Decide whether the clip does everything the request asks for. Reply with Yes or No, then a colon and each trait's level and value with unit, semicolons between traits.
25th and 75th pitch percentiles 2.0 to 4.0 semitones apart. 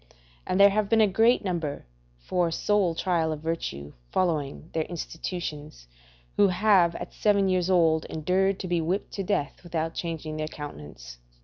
Yes: average, 3.6 semitones